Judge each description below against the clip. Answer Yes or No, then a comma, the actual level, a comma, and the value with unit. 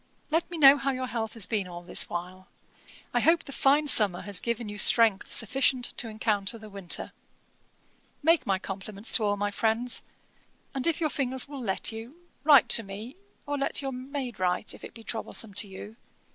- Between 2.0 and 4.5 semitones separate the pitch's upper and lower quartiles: No, average, 4.9 semitones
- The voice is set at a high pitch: Yes, high, 230 Hz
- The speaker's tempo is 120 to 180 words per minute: No, average, 195 wpm